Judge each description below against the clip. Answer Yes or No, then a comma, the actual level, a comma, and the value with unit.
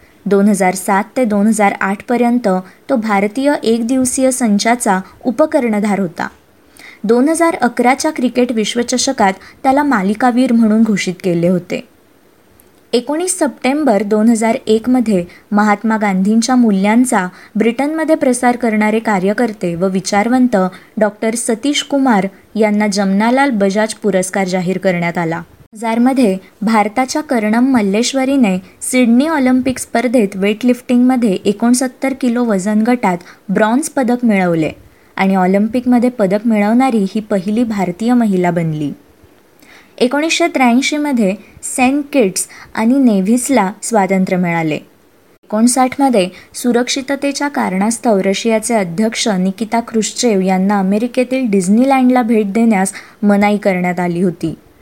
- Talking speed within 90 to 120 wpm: Yes, average, 105 wpm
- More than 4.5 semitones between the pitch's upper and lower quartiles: No, average, 4.2 semitones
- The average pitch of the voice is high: Yes, high, 225 Hz